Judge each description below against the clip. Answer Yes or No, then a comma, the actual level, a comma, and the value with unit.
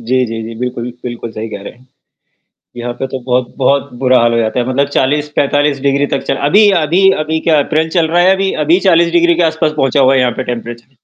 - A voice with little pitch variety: No, average, 4.4 semitones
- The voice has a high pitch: No, low, 135 Hz